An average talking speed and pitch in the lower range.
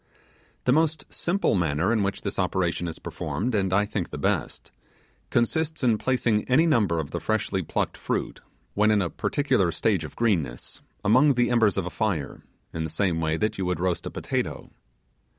Yes: average, 185 wpm; low, 100 Hz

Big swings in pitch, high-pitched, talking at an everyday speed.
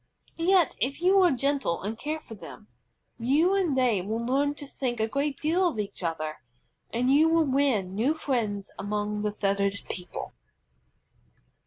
Yes: wide, 6.2 semitones; very high, 255 Hz; average, 165 wpm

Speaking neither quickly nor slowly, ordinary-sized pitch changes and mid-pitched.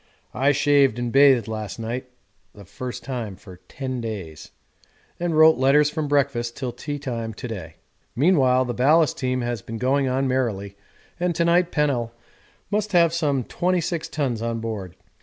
No: average, 165 wpm; average, 4.2 semitones; low, 130 Hz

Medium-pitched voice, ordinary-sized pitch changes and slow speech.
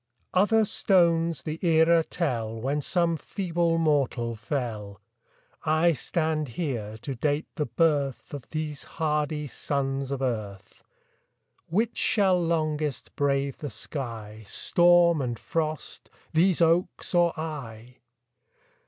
Yes: medium, 150 Hz; average, 4.4 semitones; slow, 115 wpm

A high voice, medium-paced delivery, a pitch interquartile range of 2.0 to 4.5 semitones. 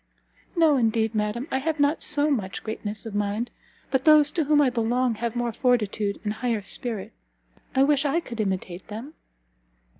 No: high, 235 Hz; average, 175 wpm; average, 4.9 semitones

